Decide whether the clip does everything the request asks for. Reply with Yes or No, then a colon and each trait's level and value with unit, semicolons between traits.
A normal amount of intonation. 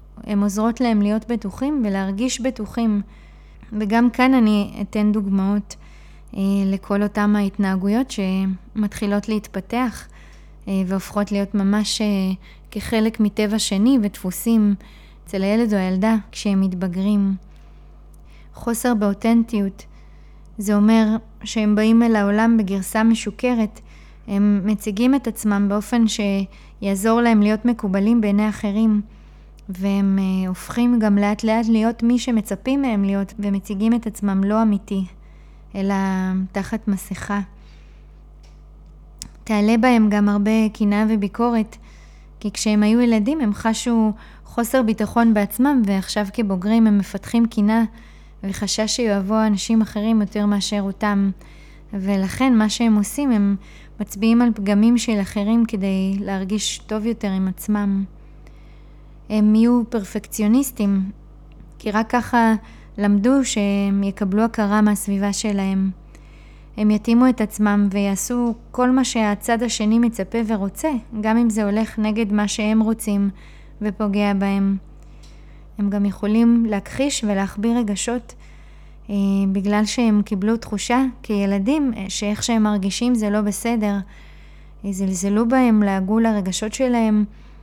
No: narrow, 2.2 semitones